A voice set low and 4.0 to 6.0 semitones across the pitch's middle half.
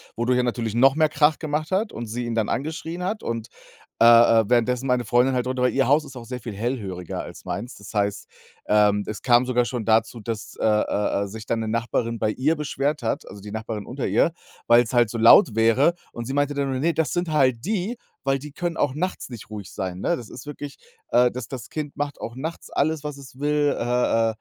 Yes: low, 125 Hz; average, 4.3 semitones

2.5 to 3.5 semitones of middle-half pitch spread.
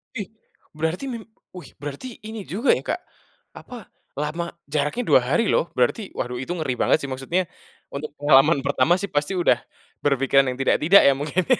No: average, 5.1 semitones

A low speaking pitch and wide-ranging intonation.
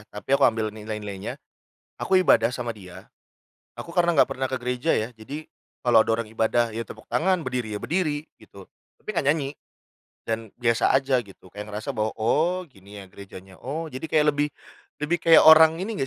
Yes: low, 125 Hz; wide, 6.2 semitones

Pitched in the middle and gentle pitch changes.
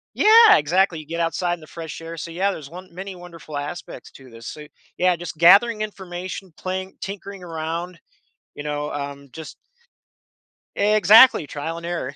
No: medium, 170 Hz; average, 3.4 semitones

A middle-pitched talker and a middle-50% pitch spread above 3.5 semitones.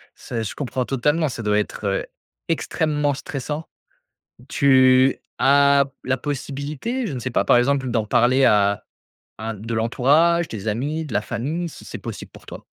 No: low, 130 Hz; average, 4.1 semitones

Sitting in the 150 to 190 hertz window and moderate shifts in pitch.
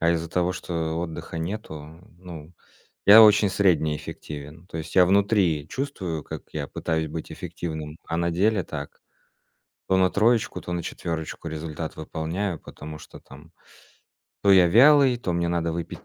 No: very low, 85 Hz; average, 3.2 semitones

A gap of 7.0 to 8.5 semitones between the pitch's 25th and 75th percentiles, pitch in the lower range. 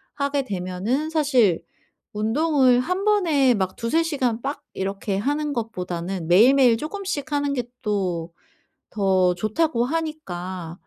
No: wide, 7.4 semitones; high, 240 Hz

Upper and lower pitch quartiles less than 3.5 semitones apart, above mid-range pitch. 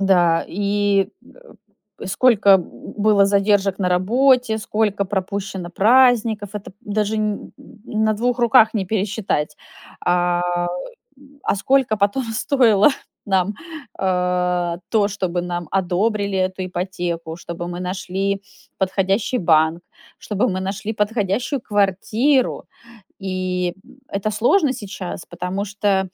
Yes: average, 2.8 semitones; high, 200 Hz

